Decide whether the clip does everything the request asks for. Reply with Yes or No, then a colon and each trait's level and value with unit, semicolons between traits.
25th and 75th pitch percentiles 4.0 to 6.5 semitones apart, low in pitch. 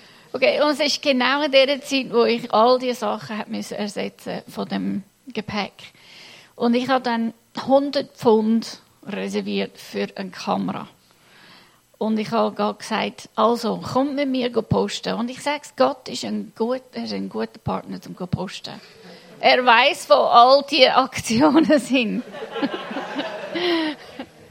No: average, 4.3 semitones; high, 235 Hz